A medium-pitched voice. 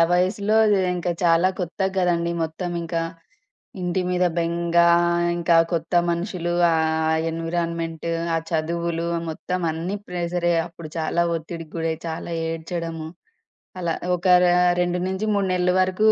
Yes: medium, 170 Hz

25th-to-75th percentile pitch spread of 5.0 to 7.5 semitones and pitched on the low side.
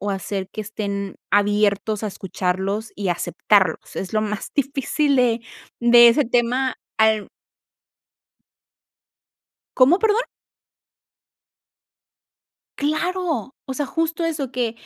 No: average, 5.3 semitones; high, 230 Hz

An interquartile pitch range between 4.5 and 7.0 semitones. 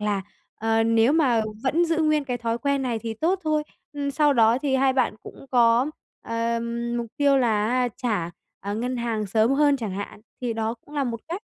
No: average, 3.9 semitones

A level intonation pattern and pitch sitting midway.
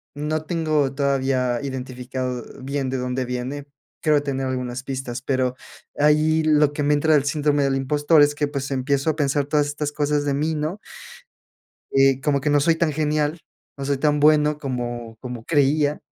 Yes: narrow, 2.1 semitones; medium, 145 Hz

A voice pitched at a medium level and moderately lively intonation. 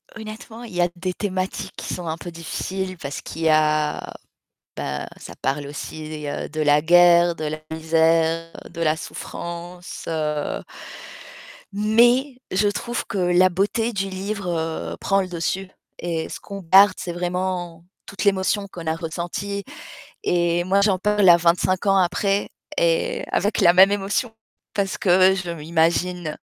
Yes: medium, 180 Hz; average, 3.2 semitones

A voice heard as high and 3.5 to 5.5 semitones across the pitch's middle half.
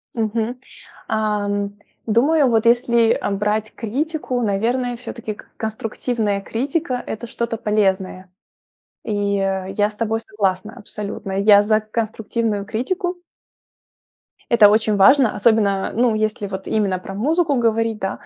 No: high, 220 Hz; narrow, 2.5 semitones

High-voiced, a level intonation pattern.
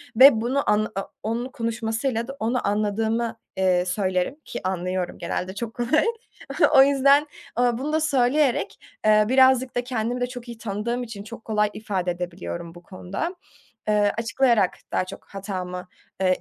No: high, 225 Hz; average, 4.4 semitones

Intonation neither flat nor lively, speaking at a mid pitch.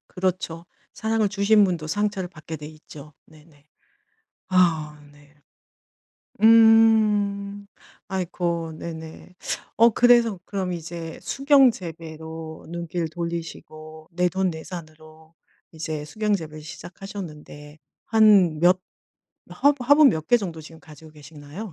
Yes: average, 4.4 semitones; medium, 170 Hz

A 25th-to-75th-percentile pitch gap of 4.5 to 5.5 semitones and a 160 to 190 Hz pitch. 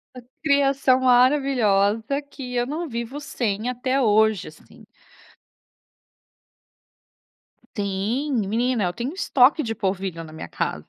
No: average, 4.8 semitones; high, 245 Hz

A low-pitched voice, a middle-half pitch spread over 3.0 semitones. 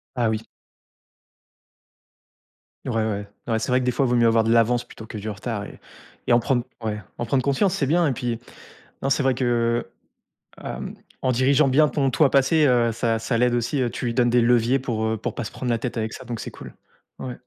No: low, 120 Hz; average, 2.7 semitones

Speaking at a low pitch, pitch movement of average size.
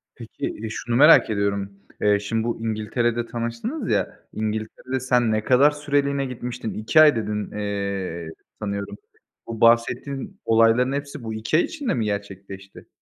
Yes: low, 115 Hz; average, 3.8 semitones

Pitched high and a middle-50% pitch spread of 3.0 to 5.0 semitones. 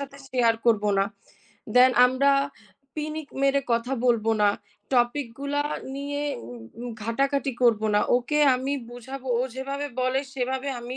No: very high, 260 Hz; narrow, 2.6 semitones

